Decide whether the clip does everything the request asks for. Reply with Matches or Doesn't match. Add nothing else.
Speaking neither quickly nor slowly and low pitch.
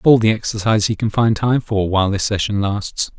Doesn't match